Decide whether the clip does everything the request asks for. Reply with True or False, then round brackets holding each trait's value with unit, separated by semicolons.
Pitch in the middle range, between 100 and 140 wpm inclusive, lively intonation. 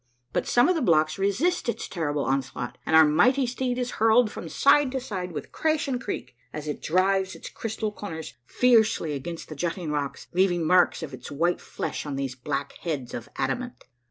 False (175 Hz; 195 wpm; 8.1 semitones)